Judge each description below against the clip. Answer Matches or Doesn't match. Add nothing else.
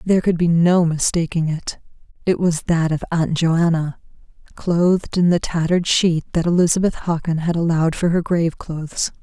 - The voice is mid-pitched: Matches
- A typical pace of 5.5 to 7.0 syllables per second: Doesn't match